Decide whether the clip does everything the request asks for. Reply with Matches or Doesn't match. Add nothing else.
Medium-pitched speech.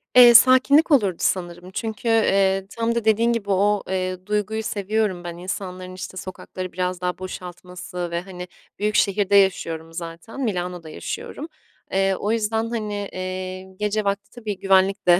Doesn't match